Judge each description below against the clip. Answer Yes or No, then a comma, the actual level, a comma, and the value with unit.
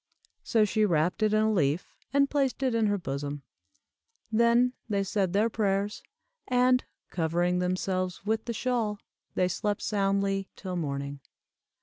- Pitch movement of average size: Yes, average, 3.7 semitones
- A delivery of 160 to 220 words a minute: No, average, 145 wpm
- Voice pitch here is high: Yes, high, 200 Hz